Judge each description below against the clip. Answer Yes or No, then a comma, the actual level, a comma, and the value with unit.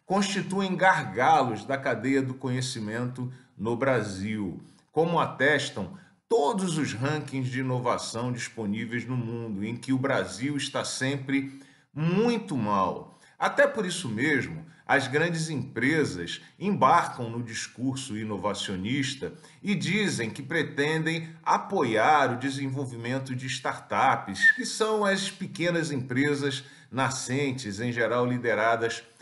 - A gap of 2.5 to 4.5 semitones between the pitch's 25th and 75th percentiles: No, average, 4.9 semitones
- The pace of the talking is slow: Yes, slow, 115 wpm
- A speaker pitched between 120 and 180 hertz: Yes, low, 135 Hz